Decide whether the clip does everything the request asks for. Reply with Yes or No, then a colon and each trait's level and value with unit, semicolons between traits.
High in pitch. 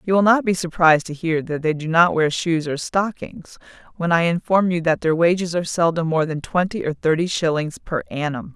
No: medium, 165 Hz